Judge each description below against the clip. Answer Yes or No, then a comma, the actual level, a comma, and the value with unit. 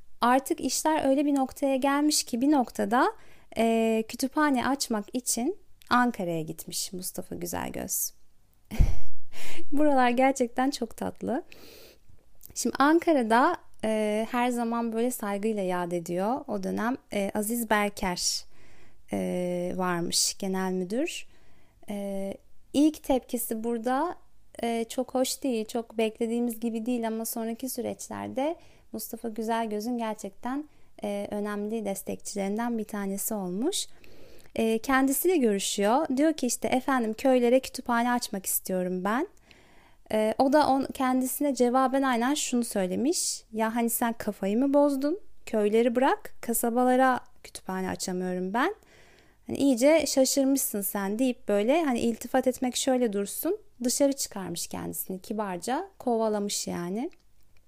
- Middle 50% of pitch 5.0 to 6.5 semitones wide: No, average, 4.5 semitones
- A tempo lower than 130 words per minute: Yes, average, 120 wpm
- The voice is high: Yes, high, 235 Hz